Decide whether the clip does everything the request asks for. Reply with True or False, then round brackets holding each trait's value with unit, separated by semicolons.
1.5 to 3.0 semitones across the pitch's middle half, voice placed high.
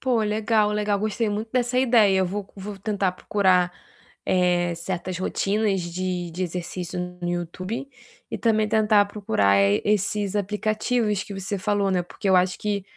True (2.6 semitones; 200 Hz)